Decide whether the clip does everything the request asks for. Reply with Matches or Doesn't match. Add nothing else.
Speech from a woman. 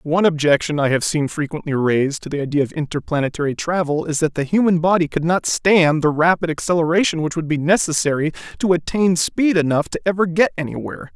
Doesn't match